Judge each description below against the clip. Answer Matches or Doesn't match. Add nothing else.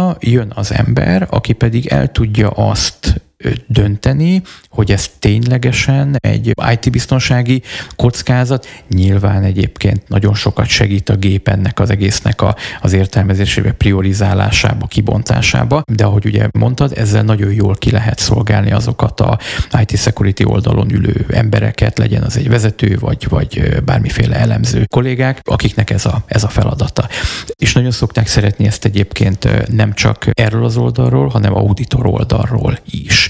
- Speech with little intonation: Doesn't match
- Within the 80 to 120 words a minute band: Doesn't match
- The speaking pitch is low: Matches